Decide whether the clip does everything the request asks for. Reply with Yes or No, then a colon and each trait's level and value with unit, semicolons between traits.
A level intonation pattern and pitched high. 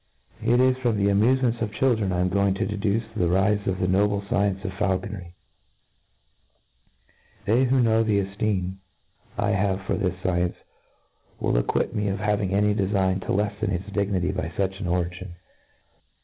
No: narrow, 2.1 semitones; low, 100 Hz